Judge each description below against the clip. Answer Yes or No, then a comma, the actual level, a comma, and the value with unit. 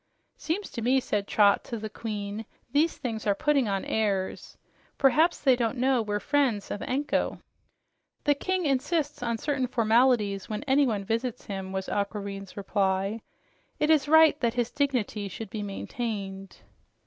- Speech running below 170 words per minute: Yes, average, 155 wpm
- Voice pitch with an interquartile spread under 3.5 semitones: No, average, 5.1 semitones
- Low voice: No, high, 230 Hz